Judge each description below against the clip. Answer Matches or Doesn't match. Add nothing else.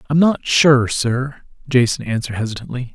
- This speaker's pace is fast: Doesn't match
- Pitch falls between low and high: Doesn't match